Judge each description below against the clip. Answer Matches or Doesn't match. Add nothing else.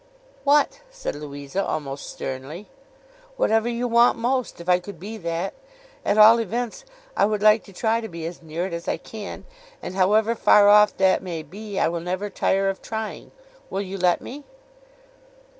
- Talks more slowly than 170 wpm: Doesn't match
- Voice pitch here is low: Doesn't match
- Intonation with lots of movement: Doesn't match